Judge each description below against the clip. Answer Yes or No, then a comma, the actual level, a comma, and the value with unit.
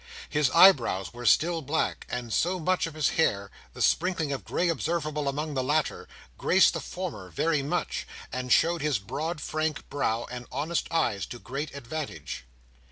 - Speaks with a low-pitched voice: No, medium, 150 Hz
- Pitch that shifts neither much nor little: Yes, average, 4.5 semitones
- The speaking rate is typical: Yes, average, 170 wpm